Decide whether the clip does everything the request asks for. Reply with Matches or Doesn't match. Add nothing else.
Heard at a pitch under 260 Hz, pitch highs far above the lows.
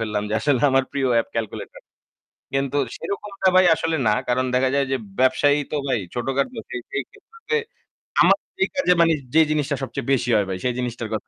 Doesn't match